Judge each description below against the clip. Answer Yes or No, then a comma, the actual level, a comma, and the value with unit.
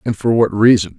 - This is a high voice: No, low, 110 Hz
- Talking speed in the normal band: No, fast, 245 wpm